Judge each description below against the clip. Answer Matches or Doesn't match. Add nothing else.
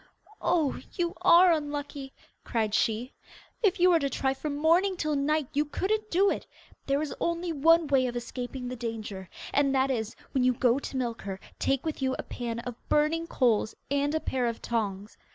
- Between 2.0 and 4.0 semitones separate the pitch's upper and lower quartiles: Doesn't match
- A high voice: Matches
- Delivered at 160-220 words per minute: Matches